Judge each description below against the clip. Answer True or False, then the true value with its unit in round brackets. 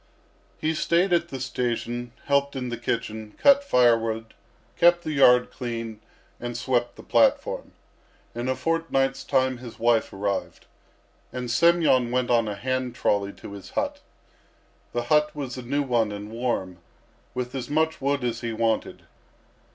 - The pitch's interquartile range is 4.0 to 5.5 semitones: False (3.3 semitones)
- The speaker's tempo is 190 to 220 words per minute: False (155 wpm)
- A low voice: True (125 Hz)